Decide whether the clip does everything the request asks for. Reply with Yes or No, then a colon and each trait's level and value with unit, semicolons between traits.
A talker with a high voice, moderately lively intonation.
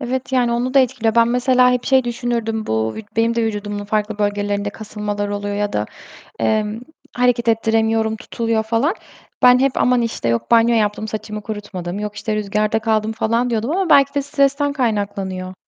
Yes: high, 225 Hz; average, 3.0 semitones